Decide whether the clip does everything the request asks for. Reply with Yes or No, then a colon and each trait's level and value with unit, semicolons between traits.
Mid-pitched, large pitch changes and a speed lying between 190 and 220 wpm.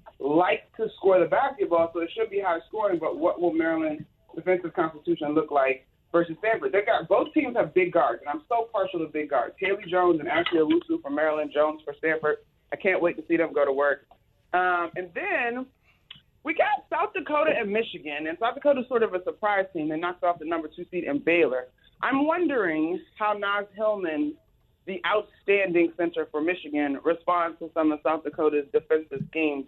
Yes: medium, 175 Hz; wide, 6.4 semitones; average, 200 wpm